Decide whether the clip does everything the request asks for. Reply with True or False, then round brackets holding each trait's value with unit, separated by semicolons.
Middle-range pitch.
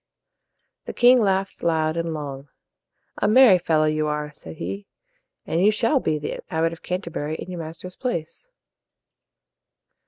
True (165 Hz)